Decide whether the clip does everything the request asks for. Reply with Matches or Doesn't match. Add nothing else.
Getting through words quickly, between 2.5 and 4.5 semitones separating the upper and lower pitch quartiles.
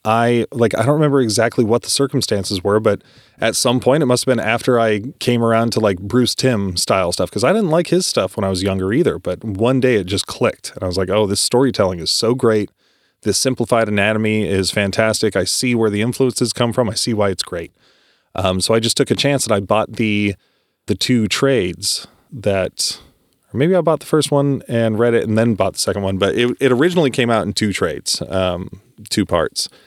Matches